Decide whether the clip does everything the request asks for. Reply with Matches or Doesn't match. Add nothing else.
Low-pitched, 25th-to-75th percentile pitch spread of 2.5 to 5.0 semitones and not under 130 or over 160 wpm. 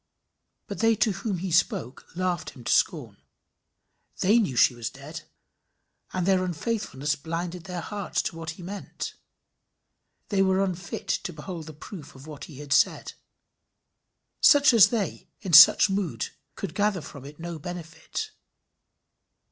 Doesn't match